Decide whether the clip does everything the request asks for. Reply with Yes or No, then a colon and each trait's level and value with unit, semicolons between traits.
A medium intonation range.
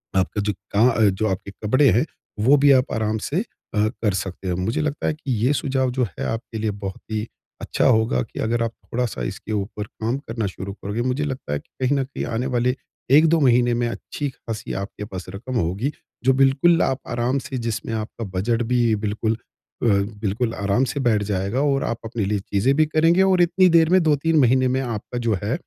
Yes: average, 4.3 semitones